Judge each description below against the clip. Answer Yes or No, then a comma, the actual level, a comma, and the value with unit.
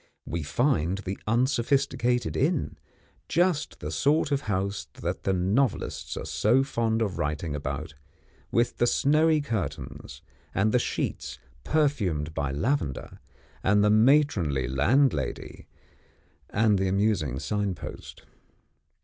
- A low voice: Yes, low, 105 Hz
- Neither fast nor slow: No, slow, 115 wpm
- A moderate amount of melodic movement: No, wide, 7.8 semitones